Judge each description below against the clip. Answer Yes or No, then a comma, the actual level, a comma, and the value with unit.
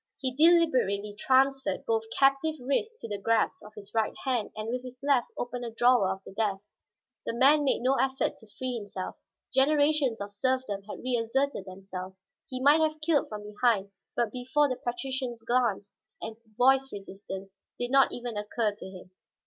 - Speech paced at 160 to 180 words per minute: Yes, average, 175 wpm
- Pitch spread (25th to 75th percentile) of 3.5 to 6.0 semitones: Yes, average, 4.4 semitones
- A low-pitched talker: No, high, 245 Hz